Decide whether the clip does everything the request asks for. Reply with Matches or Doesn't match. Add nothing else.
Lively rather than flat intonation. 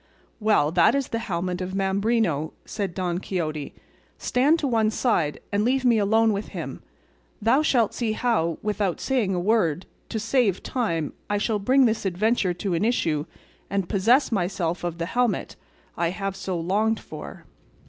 Doesn't match